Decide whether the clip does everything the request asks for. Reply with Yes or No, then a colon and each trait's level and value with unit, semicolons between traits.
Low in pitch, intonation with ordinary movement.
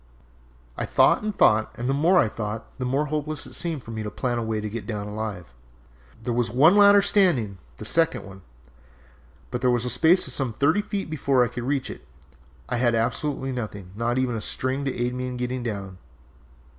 Yes: low, 125 Hz; average, 4.5 semitones